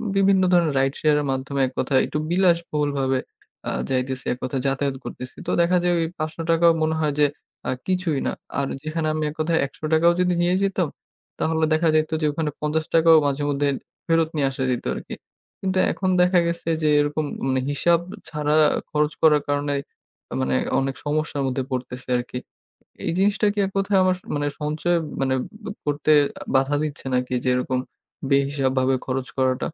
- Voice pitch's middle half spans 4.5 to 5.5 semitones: No, average, 3.5 semitones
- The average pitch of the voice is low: No, medium, 150 Hz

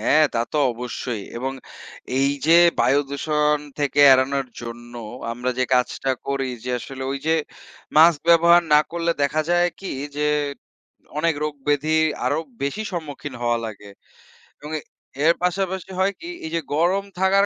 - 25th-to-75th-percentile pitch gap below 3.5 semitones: No, average, 4.3 semitones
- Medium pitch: Yes, medium, 150 Hz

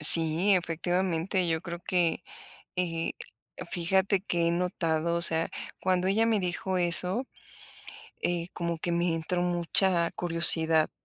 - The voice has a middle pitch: Yes, medium, 175 Hz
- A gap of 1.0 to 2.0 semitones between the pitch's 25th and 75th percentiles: Yes, narrow, 1.6 semitones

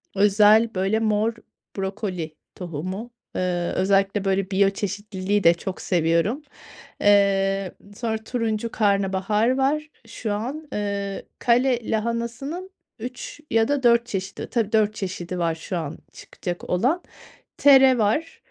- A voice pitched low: No, high, 205 Hz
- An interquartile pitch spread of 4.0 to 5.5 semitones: No, average, 3.5 semitones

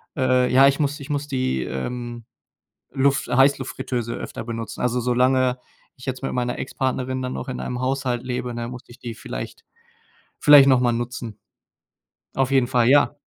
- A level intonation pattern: Yes, narrow, 1.6 semitones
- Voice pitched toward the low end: Yes, low, 125 Hz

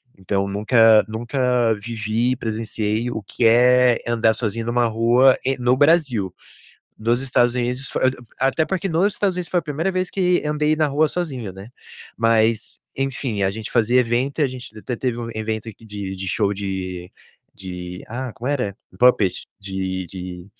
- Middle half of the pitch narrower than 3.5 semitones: No, average, 3.8 semitones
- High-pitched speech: No, low, 115 Hz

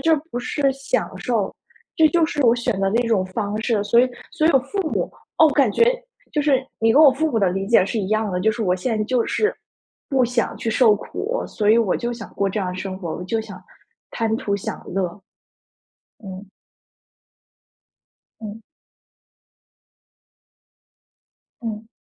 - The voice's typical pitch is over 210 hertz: Yes, high, 225 Hz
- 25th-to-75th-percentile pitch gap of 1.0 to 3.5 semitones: No, average, 4.2 semitones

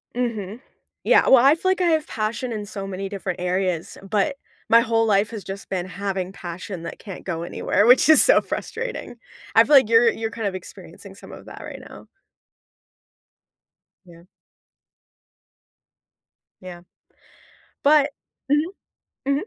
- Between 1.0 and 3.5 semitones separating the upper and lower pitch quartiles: No, wide, 5.5 semitones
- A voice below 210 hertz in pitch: No, high, 215 Hz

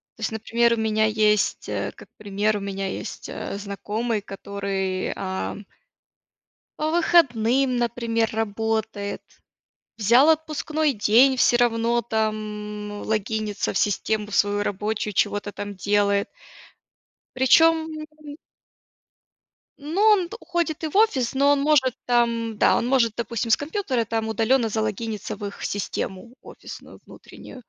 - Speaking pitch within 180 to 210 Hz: No, high, 225 Hz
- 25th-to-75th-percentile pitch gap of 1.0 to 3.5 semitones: No, average, 4.1 semitones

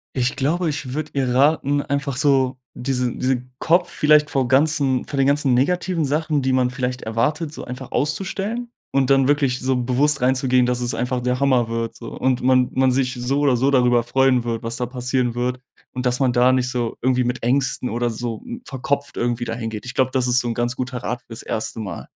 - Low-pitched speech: Yes, low, 130 Hz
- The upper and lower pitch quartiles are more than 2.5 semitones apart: No, narrow, 2.2 semitones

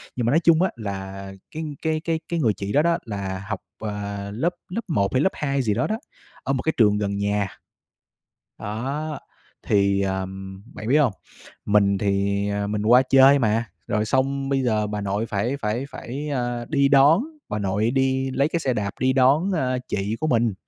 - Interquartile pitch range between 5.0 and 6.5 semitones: Yes, average, 5.3 semitones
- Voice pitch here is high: No, low, 115 Hz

